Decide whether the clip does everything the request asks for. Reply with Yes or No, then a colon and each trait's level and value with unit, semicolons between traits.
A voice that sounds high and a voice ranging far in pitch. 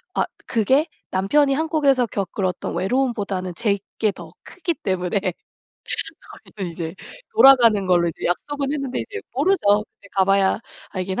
Yes: high, 210 Hz; wide, 6.5 semitones